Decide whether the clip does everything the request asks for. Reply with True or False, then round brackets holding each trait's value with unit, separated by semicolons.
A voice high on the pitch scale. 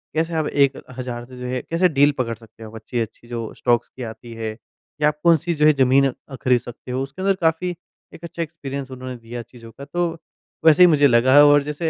False (135 Hz)